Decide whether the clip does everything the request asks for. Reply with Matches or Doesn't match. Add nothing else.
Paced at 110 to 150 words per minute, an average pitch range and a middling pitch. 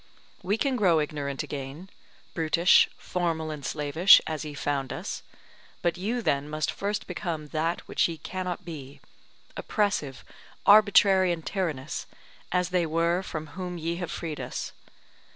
Matches